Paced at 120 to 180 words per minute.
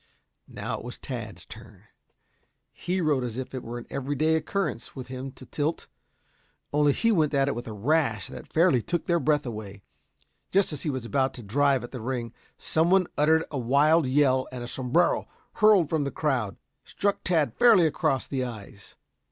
No: average, 190 wpm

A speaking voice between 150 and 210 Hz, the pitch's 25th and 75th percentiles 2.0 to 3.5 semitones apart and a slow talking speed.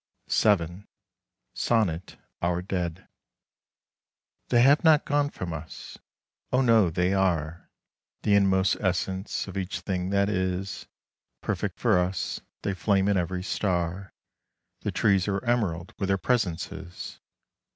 No: very low, 95 Hz; narrow, 2.4 semitones; slow, 125 wpm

